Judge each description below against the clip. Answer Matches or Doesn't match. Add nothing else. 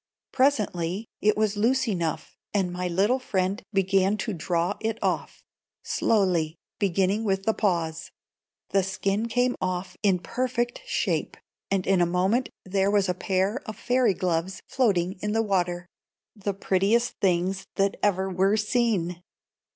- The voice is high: Matches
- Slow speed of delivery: Doesn't match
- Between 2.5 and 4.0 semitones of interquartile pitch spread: Matches